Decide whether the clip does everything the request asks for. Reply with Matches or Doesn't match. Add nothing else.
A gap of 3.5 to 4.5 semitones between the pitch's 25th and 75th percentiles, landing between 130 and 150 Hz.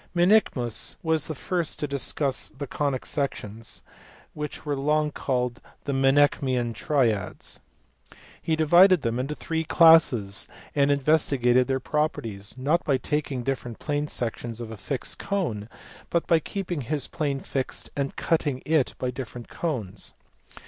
Matches